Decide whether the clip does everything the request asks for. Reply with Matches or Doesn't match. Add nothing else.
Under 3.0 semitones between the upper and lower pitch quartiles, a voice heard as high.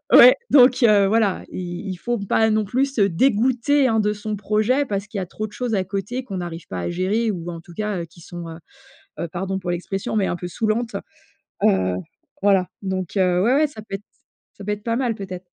Doesn't match